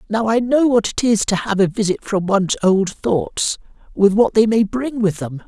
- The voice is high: Yes, high, 210 Hz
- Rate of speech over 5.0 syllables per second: No, 4.7 syllables/s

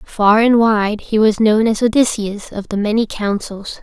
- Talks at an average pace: Yes, average, 190 wpm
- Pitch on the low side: No, high, 215 Hz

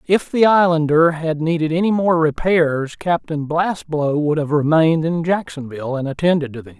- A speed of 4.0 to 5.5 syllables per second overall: Yes, 5.0 syllables/s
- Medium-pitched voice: Yes, medium, 155 Hz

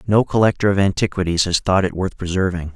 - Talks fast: No, average, 195 wpm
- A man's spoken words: Yes, male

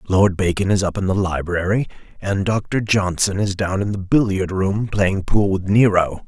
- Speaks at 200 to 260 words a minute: No, average, 190 wpm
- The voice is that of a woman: No, male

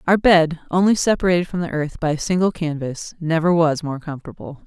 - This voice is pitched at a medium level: Yes, medium, 165 Hz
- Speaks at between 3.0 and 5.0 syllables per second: No, 5.8 syllables/s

